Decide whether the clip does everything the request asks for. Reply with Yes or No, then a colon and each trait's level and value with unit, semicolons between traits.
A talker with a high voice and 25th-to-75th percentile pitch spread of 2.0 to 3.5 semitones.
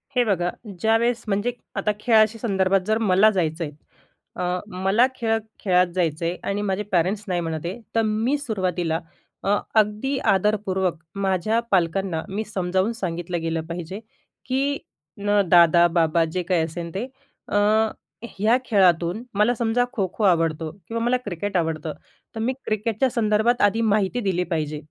No: high, 195 Hz; average, 4.1 semitones